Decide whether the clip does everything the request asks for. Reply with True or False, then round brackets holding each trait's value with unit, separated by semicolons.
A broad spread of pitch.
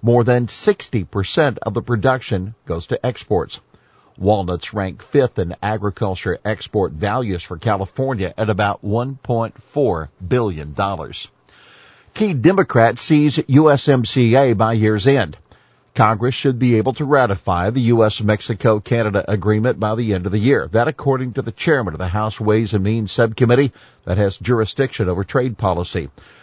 False (4.2 semitones)